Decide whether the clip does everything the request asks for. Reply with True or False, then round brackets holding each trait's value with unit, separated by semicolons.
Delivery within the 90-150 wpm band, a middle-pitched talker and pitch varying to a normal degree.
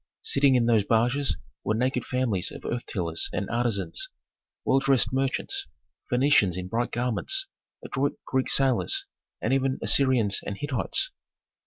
False (140 wpm; 125 Hz; 3.5 semitones)